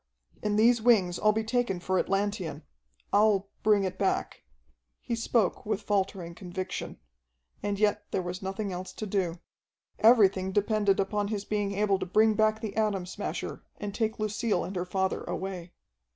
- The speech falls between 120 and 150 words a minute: No, average, 165 wpm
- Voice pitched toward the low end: No, high, 200 Hz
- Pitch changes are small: Yes, narrow, 2.2 semitones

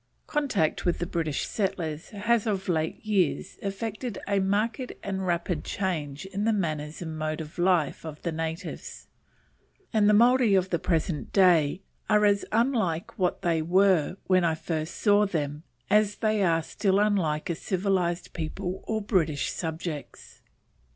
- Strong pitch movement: No, average, 4.1 semitones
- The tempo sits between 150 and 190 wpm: Yes, average, 155 wpm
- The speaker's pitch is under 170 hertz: No, medium, 185 Hz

